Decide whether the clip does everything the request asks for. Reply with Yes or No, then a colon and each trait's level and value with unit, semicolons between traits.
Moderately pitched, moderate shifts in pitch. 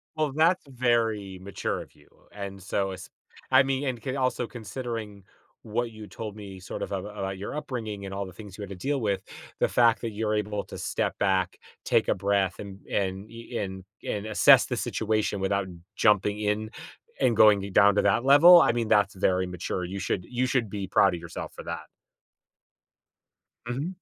No: low, 105 Hz; average, 3.4 semitones